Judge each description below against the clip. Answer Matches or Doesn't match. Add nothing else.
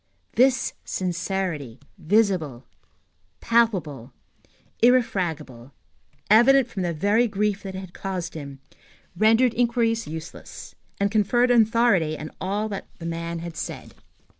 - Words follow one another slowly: Matches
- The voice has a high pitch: Matches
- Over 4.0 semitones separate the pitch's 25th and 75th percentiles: Matches